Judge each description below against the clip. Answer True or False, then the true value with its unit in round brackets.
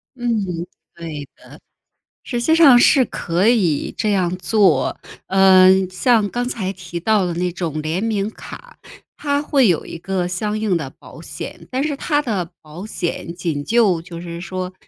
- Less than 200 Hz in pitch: True (190 Hz)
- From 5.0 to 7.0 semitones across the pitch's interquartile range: True (5.3 semitones)